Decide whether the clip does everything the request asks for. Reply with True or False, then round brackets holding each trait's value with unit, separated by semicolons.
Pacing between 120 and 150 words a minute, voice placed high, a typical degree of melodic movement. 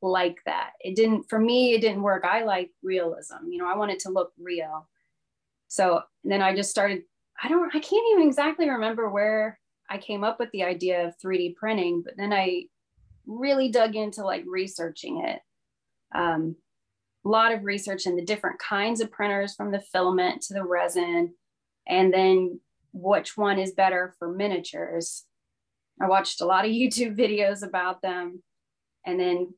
False (180 wpm; 195 Hz; 3.6 semitones)